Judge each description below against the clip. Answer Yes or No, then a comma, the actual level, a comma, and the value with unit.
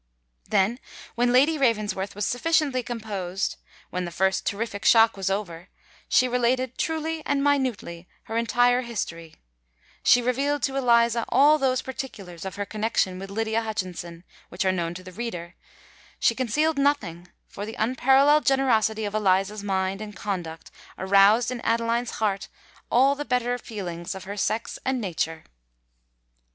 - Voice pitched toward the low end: No, high, 220 Hz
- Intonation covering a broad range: No, average, 4.8 semitones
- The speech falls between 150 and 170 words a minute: No, average, 140 wpm